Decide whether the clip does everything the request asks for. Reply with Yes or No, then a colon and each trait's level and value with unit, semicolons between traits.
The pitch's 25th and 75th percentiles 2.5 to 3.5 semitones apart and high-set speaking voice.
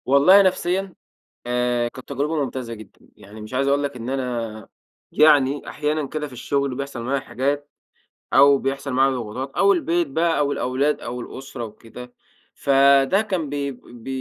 No: average, 2.9 semitones; low, 135 Hz